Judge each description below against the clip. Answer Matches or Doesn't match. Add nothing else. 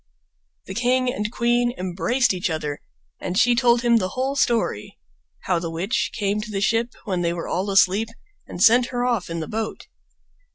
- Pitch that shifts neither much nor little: Matches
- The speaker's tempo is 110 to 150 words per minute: Doesn't match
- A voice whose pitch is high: Matches